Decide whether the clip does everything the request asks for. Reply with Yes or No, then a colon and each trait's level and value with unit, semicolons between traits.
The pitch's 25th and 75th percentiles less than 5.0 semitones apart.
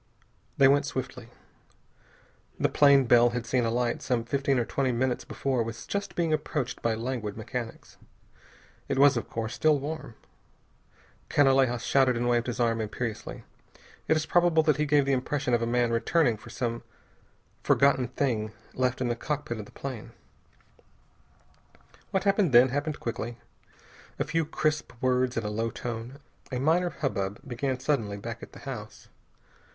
Yes: average, 3.4 semitones